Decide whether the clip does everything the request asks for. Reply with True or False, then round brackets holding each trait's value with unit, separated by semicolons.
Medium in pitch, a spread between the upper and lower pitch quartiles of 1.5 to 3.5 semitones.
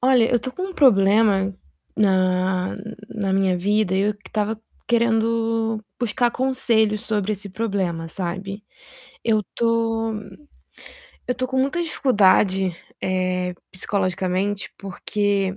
False (205 Hz; 3.2 semitones)